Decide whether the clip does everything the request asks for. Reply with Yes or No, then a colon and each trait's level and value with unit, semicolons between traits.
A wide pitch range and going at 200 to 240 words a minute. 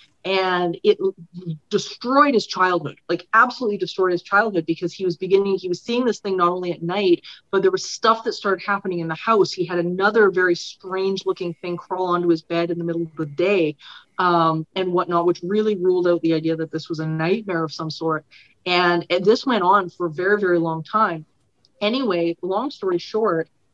No: average, 2.8 semitones; fast, 205 wpm